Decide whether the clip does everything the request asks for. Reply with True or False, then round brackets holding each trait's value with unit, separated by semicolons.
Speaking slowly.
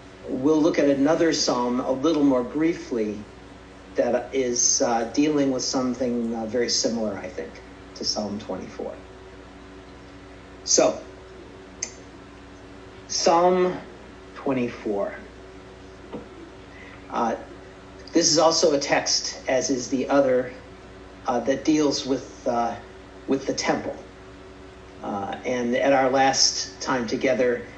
True (115 wpm)